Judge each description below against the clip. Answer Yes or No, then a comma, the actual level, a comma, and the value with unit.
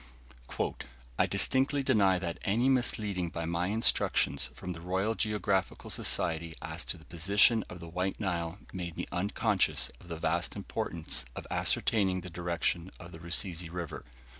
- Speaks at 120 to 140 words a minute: No, average, 155 wpm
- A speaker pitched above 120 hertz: No, very low, 90 Hz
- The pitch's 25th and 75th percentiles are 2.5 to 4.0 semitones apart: Yes, average, 3.3 semitones